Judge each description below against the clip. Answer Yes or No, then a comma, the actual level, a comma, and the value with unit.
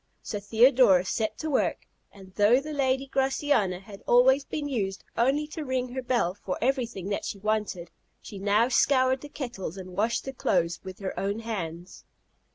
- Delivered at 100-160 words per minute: No, average, 175 wpm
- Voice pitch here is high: Yes, high, 225 Hz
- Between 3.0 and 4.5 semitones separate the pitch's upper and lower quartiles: No, average, 5.3 semitones